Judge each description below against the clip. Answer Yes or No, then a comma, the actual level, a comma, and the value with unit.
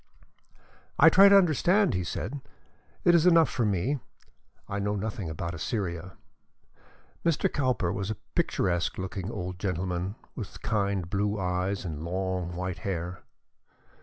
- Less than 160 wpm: Yes, average, 140 wpm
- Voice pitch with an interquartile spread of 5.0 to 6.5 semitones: No, average, 4.0 semitones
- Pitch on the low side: Yes, very low, 95 Hz